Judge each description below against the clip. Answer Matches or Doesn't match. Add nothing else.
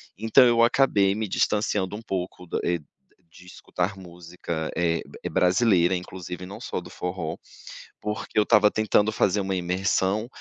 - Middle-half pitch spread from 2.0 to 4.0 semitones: Matches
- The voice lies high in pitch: Doesn't match